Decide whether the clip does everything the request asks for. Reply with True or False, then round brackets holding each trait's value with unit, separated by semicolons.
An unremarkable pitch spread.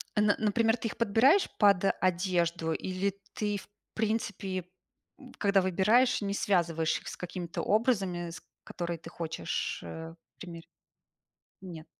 True (3.6 semitones)